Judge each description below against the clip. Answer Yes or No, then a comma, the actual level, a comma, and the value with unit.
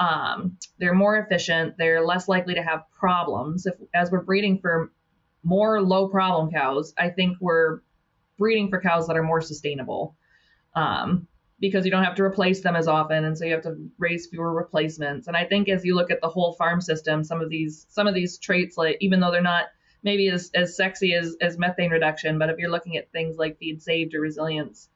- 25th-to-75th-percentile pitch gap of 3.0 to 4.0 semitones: No, narrow, 2.4 semitones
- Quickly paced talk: Yes, fast, 215 wpm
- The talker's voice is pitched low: No, medium, 170 Hz